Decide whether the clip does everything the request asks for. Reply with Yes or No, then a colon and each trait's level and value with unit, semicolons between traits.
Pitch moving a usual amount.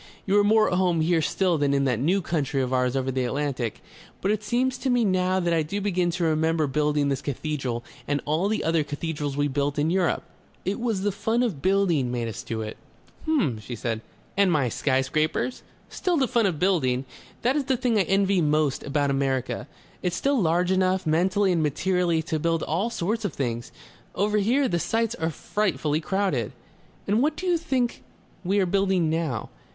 No: wide, 5.8 semitones